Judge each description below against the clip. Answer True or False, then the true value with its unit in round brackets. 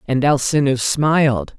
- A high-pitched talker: False (140 Hz)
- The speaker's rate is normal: False (115 wpm)